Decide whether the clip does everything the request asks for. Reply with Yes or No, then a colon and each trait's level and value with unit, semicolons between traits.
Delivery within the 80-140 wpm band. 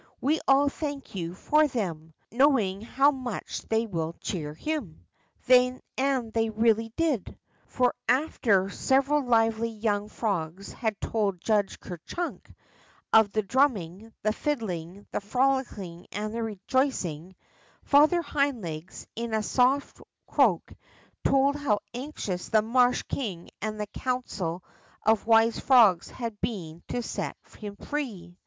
Yes: slow, 135 wpm